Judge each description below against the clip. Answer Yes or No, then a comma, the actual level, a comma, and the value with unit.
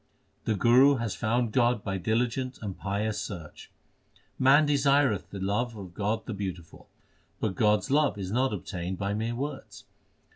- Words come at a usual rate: Yes, average, 160 wpm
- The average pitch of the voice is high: No, low, 110 Hz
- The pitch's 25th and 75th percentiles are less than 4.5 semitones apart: Yes, average, 4.0 semitones